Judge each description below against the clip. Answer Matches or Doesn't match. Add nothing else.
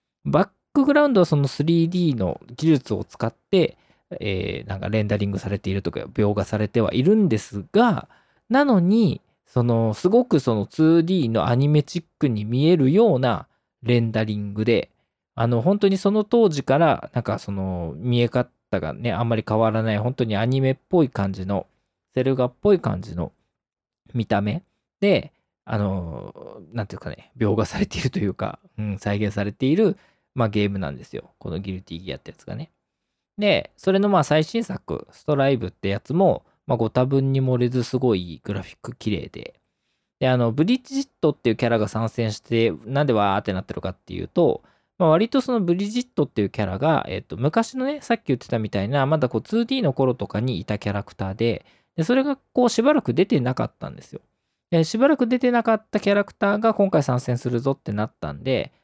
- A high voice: Doesn't match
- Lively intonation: Matches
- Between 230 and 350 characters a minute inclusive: Doesn't match